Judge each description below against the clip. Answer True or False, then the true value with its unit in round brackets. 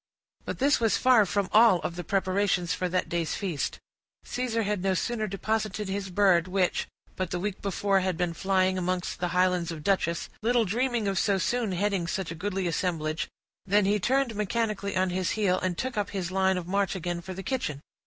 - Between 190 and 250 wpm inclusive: True (205 wpm)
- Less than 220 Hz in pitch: True (190 Hz)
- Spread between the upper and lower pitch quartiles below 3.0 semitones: True (2.6 semitones)